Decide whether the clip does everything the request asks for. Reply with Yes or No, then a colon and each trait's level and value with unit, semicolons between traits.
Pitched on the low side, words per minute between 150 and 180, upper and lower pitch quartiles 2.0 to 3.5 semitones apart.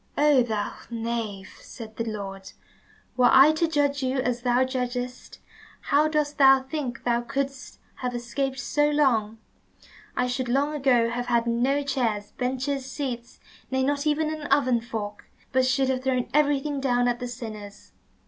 No: very high, 255 Hz; average, 160 wpm; average, 2.8 semitones